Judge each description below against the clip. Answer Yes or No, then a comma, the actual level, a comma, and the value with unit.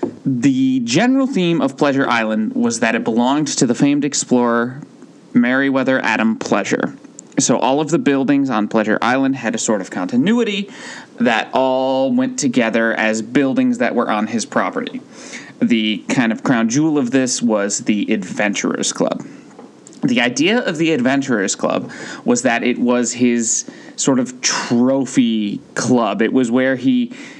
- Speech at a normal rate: Yes, average, 155 wpm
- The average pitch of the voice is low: No, medium, 145 Hz